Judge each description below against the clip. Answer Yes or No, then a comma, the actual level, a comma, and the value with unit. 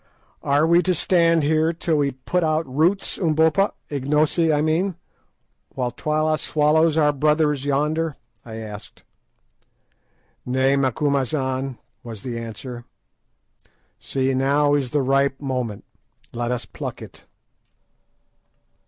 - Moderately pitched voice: Yes, medium, 145 Hz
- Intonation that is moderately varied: Yes, average, 3.3 semitones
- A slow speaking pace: Yes, slow, 110 wpm